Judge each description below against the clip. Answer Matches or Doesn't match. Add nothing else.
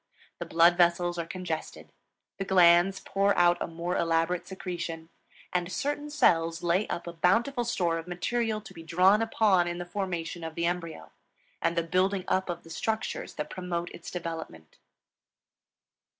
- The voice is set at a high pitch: Doesn't match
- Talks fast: Doesn't match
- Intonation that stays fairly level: Matches